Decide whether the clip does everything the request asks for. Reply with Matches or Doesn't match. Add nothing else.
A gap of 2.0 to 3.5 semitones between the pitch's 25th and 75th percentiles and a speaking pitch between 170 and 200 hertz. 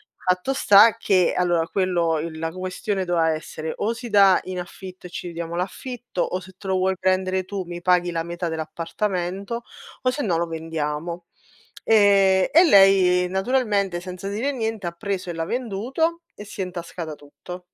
Matches